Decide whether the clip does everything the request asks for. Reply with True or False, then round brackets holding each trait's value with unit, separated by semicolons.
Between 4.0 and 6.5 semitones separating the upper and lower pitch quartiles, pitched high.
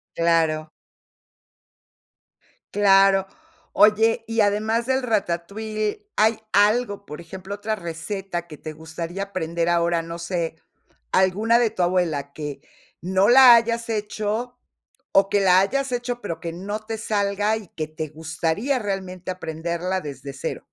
True (4.4 semitones; 195 Hz)